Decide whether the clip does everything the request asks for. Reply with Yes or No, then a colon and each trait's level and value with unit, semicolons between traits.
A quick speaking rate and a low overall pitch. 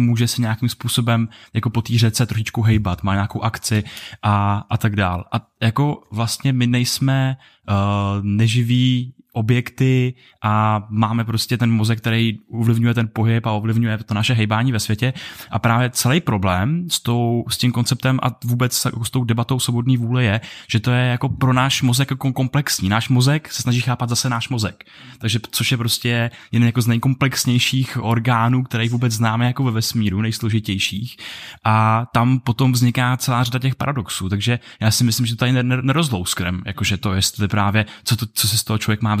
Yes: fast, 180 wpm; low, 115 Hz